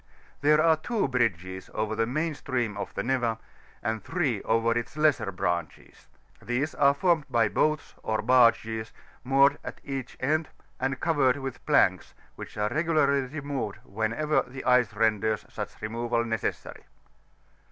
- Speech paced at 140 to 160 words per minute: Yes, average, 145 wpm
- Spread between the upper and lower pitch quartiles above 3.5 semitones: Yes, average, 4.4 semitones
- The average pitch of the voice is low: Yes, low, 125 Hz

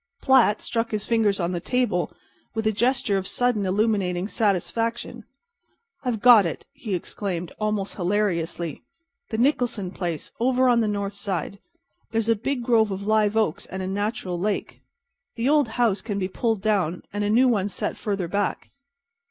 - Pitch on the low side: No, high, 210 Hz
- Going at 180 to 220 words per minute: No, average, 165 wpm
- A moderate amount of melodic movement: Yes, average, 3.3 semitones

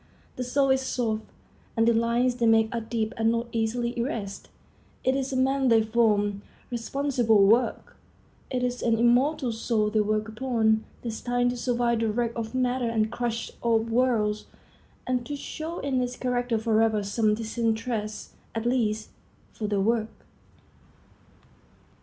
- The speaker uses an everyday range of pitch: No, narrow, 2.1 semitones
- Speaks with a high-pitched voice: Yes, high, 230 Hz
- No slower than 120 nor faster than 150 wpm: No, average, 160 wpm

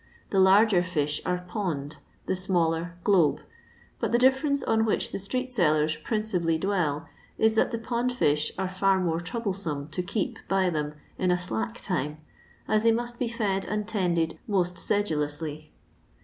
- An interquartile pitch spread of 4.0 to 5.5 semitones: Yes, average, 5.0 semitones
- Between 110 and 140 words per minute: No, average, 165 wpm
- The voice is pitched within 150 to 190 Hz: Yes, medium, 185 Hz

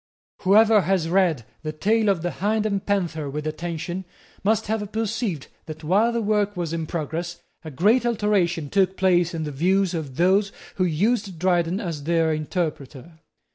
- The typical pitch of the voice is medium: Yes, medium, 180 Hz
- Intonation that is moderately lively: Yes, average, 4.1 semitones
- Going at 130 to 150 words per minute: No, average, 170 wpm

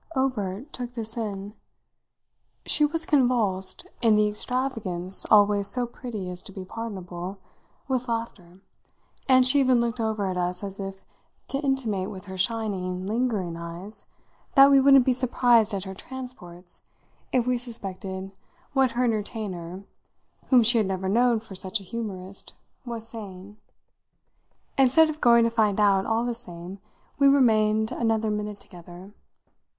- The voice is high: Yes, high, 215 Hz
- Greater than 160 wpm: No, average, 150 wpm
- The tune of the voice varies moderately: Yes, average, 4.3 semitones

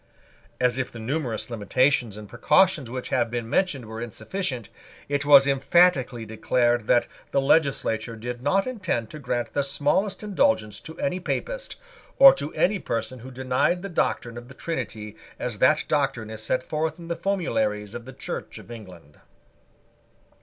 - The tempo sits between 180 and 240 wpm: No, average, 165 wpm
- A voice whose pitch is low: Yes, low, 130 Hz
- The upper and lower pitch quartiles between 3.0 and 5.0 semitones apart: No, wide, 5.6 semitones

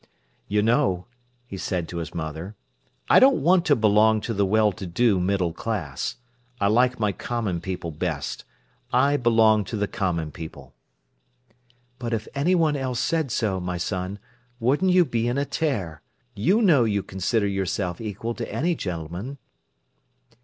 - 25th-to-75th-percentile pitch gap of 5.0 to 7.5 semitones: Yes, wide, 5.5 semitones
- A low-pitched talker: Yes, low, 105 Hz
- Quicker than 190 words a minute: No, average, 160 wpm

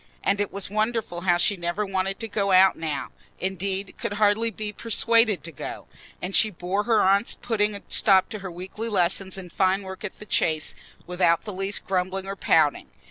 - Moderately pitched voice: No, high, 195 Hz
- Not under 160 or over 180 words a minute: No, average, 190 wpm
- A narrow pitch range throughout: Yes, narrow, 2.2 semitones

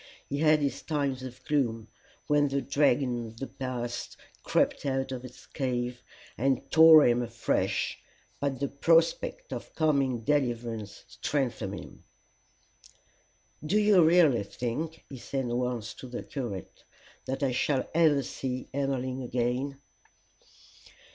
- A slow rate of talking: Yes, slow, 130 wpm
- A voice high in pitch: No, low, 130 Hz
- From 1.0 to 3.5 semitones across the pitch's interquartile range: Yes, average, 3.0 semitones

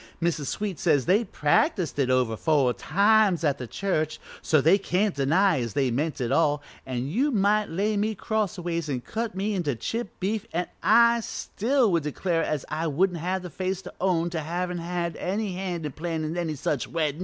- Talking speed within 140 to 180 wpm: No, average, 195 wpm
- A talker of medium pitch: Yes, medium, 175 Hz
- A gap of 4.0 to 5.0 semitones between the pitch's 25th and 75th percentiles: Yes, average, 4.7 semitones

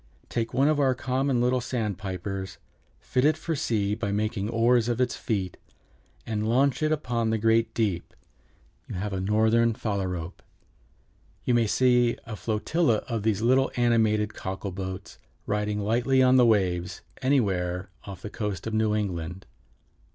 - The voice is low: Yes, low, 110 Hz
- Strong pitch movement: No, average, 3.5 semitones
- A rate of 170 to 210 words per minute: No, average, 155 wpm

